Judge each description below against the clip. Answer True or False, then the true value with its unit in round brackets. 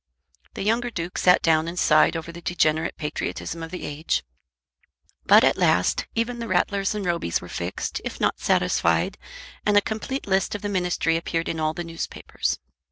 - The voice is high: False (170 Hz)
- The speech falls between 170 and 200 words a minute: True (180 wpm)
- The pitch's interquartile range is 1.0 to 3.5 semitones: False (4.0 semitones)